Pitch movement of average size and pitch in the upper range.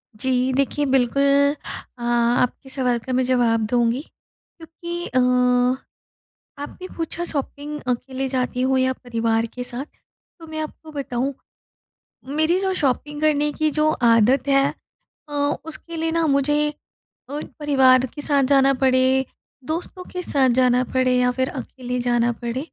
Yes: average, 3.0 semitones; very high, 265 Hz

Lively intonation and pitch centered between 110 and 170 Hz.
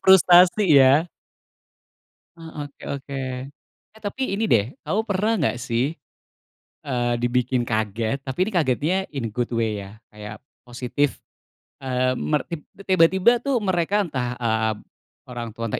Yes: wide, 6.8 semitones; low, 135 Hz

